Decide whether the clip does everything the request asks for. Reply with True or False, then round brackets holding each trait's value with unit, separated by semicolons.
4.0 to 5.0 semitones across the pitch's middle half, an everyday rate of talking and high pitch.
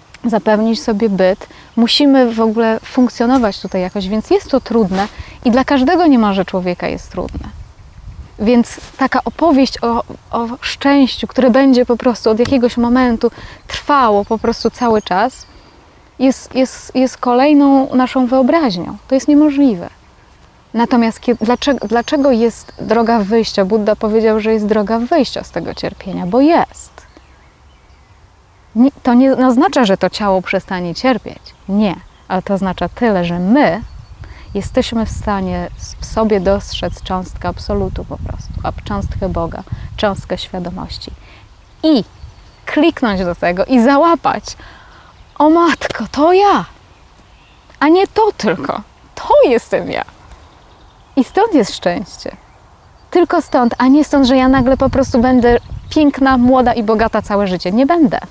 True (4.5 semitones; 140 wpm; 235 Hz)